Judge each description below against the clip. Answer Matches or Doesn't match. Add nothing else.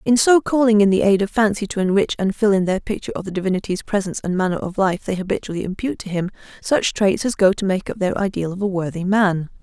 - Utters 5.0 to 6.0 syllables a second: Doesn't match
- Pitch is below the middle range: Doesn't match